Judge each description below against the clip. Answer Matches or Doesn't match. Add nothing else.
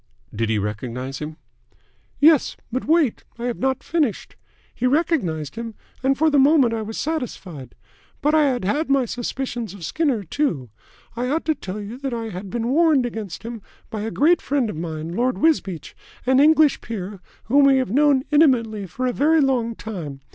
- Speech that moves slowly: Doesn't match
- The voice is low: Doesn't match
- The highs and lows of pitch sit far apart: Matches